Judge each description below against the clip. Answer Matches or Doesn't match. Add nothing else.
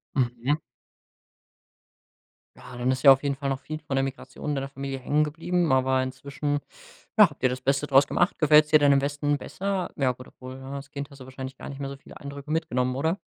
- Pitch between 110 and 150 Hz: Matches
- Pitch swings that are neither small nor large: Doesn't match